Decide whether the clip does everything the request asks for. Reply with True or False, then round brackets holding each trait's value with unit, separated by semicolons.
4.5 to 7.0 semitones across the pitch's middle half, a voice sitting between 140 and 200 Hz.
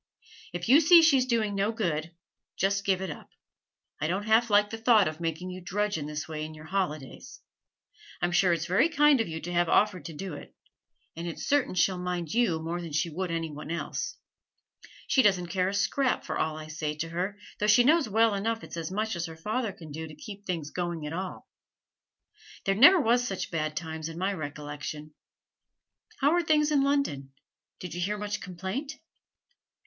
True (5.3 semitones; 185 Hz)